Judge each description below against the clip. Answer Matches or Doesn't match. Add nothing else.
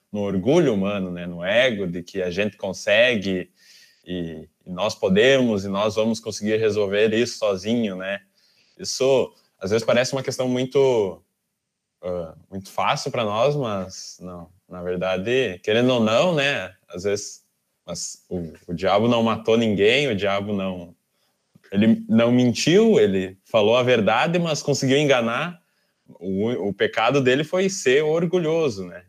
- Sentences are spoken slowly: Doesn't match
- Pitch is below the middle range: Matches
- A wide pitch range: Matches